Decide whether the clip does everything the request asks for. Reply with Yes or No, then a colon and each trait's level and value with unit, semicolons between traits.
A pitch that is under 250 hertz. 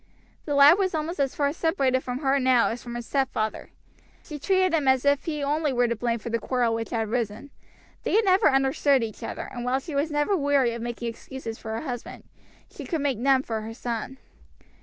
No: very high, 265 Hz